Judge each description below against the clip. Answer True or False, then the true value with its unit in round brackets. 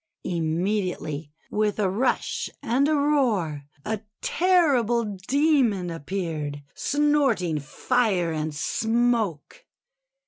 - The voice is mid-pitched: False (210 Hz)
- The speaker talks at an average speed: False (95 wpm)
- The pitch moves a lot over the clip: True (7.6 semitones)